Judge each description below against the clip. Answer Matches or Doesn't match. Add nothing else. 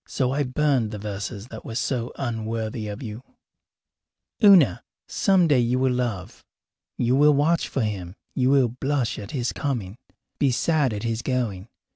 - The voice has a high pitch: Doesn't match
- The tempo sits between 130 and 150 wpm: Doesn't match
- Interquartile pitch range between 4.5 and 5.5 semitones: Doesn't match